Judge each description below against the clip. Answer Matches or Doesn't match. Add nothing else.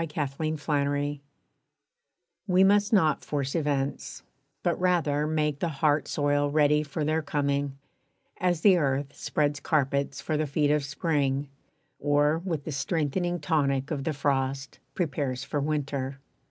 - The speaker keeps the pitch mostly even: Matches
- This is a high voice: Doesn't match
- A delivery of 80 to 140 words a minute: Matches